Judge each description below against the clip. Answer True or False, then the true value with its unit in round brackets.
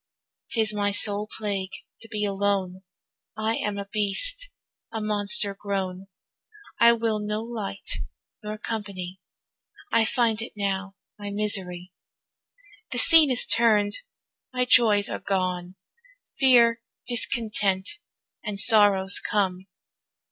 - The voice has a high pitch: True (210 Hz)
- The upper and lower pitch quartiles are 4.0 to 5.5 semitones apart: False (2.4 semitones)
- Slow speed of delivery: True (115 wpm)